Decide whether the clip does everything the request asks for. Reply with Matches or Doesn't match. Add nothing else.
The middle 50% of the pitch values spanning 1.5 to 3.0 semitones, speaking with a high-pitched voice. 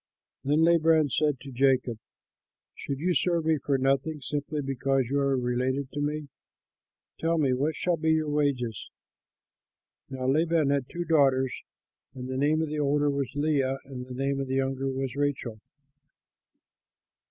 Doesn't match